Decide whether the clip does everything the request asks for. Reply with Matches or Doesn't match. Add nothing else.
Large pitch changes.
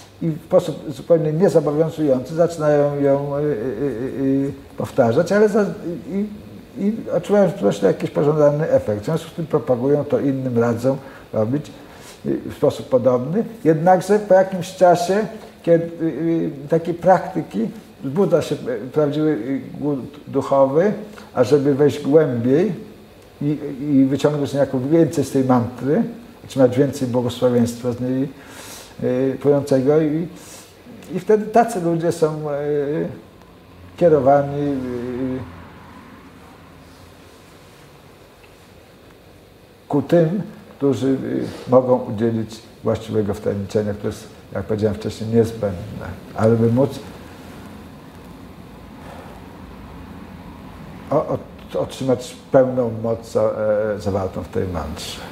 Matches